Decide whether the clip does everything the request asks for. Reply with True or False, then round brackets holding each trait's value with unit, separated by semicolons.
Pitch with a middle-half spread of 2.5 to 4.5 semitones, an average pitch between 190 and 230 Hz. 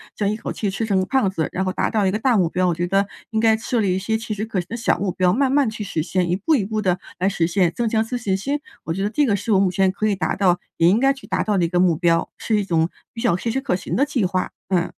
True (3.5 semitones; 200 Hz)